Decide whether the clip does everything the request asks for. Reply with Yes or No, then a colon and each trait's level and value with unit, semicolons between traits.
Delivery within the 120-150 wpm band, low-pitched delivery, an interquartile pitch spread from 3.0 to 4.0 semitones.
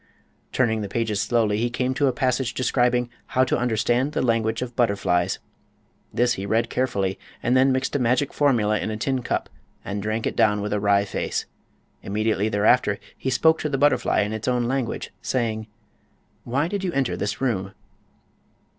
No: average, 180 wpm; low, 120 Hz; average, 3.6 semitones